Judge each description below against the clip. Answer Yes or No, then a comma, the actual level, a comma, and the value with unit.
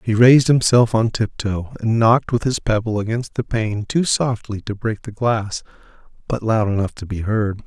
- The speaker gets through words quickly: No, average, 195 wpm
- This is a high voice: No, low, 110 Hz